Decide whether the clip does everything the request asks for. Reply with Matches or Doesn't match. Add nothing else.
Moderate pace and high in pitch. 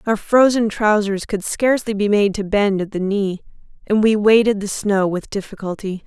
Matches